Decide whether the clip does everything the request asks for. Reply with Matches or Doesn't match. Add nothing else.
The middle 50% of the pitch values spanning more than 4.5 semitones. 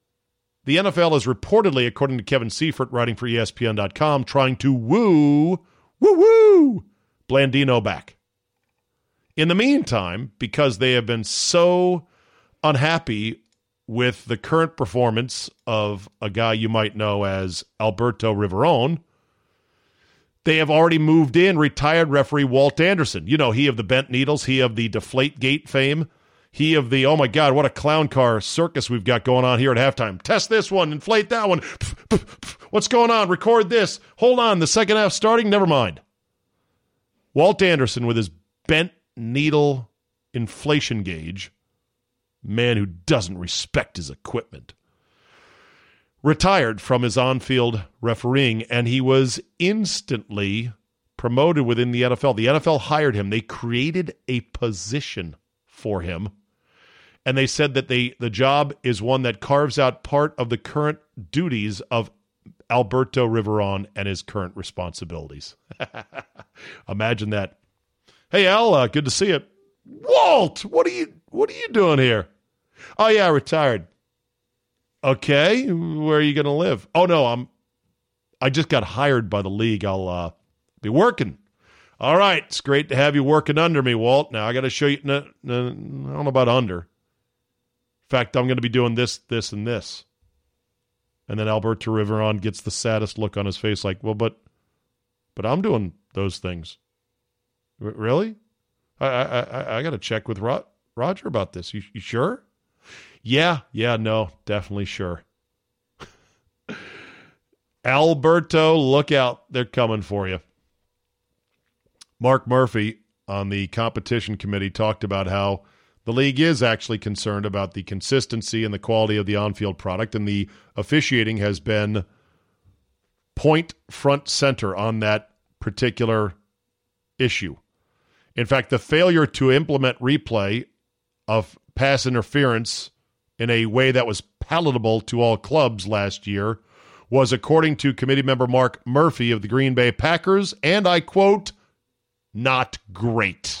Matches